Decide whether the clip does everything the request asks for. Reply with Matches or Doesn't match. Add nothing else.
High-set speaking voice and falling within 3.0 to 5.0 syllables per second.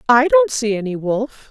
Matches